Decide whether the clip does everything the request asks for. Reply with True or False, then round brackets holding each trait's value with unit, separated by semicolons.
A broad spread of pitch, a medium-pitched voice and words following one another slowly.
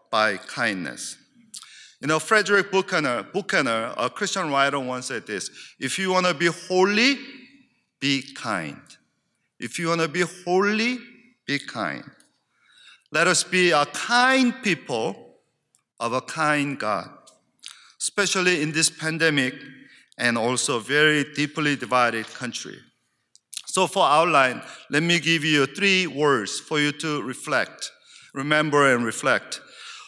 True (5.7 semitones; 165 Hz; 130 wpm)